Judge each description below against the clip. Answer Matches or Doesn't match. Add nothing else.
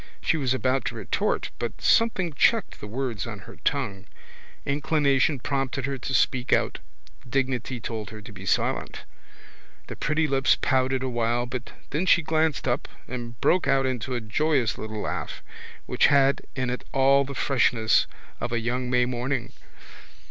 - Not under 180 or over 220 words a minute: Doesn't match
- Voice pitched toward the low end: Matches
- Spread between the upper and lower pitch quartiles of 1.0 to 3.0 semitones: Matches